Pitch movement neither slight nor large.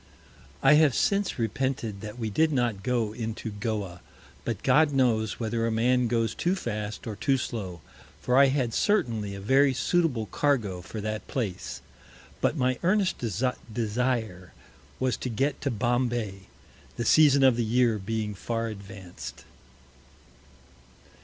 Yes: average, 3.6 semitones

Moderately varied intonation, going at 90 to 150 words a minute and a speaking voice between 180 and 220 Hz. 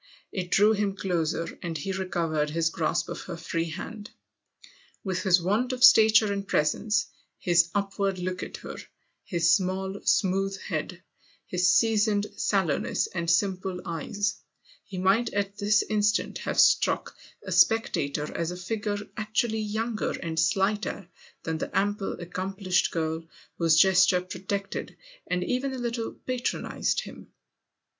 Yes: average, 3.4 semitones; average, 140 wpm; high, 190 Hz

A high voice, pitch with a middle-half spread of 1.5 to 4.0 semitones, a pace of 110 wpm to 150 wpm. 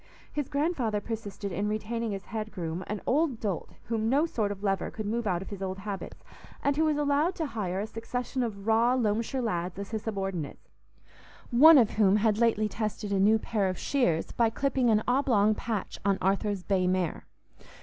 No: high, 215 Hz; average, 3.4 semitones; average, 195 wpm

